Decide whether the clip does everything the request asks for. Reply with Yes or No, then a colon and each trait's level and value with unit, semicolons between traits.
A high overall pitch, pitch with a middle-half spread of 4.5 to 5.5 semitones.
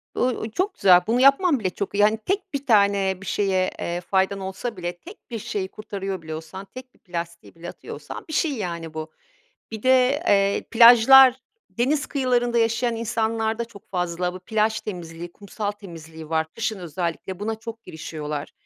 Yes: high, 205 Hz; average, 4.8 semitones